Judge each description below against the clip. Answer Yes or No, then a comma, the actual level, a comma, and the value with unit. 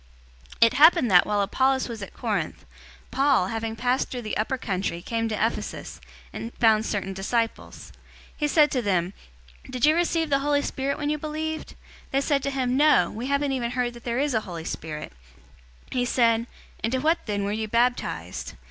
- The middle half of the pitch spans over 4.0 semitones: Yes, average, 4.4 semitones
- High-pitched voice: Yes, high, 245 Hz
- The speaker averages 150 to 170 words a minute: No, average, 195 wpm